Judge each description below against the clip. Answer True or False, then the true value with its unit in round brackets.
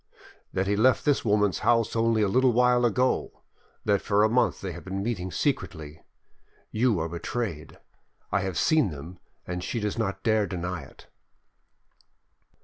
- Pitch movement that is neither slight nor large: True (4.6 semitones)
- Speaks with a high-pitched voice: False (105 Hz)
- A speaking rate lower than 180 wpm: True (165 wpm)